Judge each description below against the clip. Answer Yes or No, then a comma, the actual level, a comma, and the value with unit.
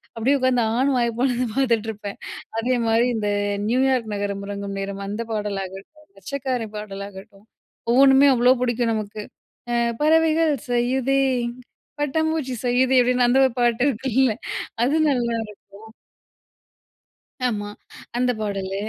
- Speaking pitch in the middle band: No, high, 240 Hz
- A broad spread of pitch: No, average, 3.9 semitones